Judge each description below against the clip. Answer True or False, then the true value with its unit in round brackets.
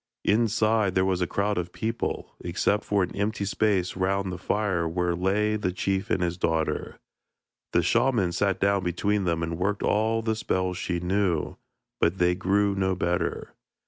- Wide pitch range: False (2.7 semitones)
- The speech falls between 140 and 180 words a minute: True (175 wpm)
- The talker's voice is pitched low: True (95 Hz)